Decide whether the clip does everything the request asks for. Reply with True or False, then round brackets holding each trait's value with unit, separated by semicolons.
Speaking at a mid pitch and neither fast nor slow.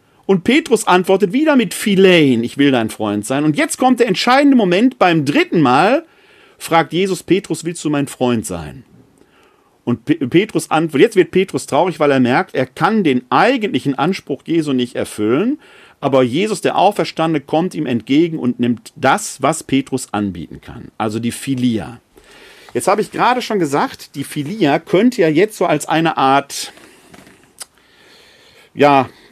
True (160 Hz; 160 wpm)